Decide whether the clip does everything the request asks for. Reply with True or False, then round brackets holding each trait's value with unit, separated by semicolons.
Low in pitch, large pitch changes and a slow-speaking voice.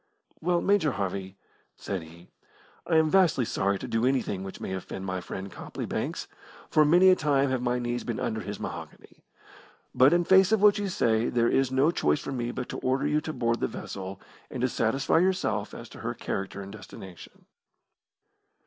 False (125 Hz; 7.7 semitones; 195 wpm)